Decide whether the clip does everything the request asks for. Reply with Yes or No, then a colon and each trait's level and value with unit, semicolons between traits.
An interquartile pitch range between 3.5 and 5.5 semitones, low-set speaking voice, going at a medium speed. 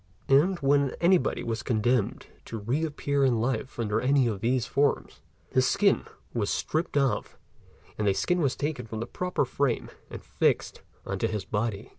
Yes: average, 4.1 semitones; low, 130 Hz; average, 180 wpm